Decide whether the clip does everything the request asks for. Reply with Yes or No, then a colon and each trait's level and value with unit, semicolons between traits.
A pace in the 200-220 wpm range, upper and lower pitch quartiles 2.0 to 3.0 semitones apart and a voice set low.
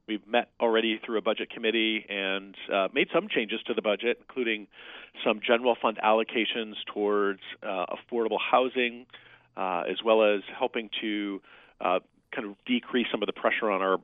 No: average, 170 wpm; narrow, 2.5 semitones; low, 110 Hz